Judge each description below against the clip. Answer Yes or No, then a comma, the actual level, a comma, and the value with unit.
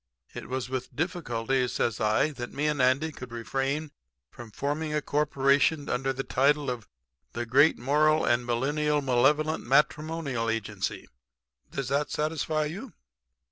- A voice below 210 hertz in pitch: Yes, medium, 140 Hz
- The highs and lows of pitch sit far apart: No, average, 3.5 semitones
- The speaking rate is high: No, average, 140 wpm